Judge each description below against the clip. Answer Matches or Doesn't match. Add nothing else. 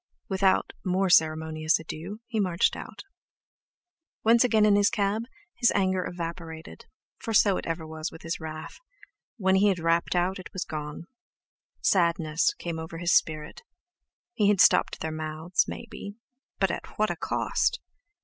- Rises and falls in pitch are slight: Doesn't match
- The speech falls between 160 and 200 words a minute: Doesn't match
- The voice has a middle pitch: Matches